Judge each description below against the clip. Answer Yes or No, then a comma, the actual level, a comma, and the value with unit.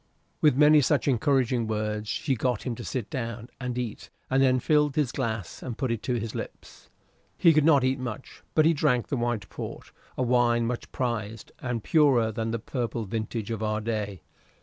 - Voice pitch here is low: Yes, low, 120 Hz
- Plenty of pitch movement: No, average, 3.1 semitones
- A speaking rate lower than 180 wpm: No, average, 195 wpm